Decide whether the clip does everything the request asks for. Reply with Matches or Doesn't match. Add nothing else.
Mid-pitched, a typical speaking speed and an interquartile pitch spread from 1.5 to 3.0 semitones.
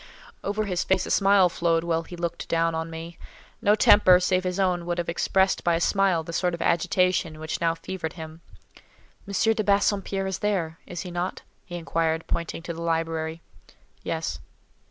Matches